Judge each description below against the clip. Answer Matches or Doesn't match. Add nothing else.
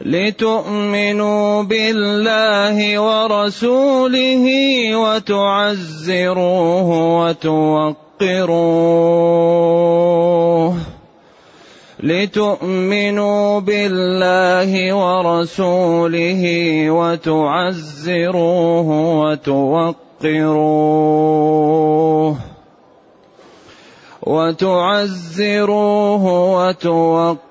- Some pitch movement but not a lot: Matches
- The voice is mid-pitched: Matches